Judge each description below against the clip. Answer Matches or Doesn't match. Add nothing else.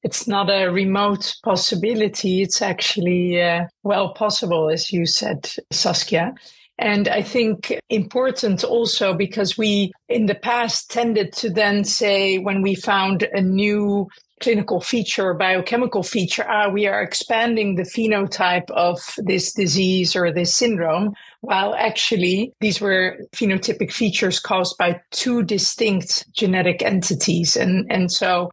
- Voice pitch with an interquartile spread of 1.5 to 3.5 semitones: Matches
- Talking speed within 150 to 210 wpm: Doesn't match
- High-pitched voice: Matches